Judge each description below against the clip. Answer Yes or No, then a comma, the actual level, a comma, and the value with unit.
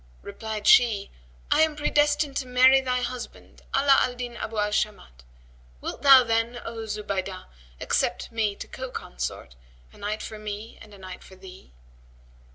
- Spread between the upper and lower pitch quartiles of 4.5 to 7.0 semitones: No, average, 3.8 semitones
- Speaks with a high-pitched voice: Yes, high, 225 Hz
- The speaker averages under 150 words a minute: No, average, 165 wpm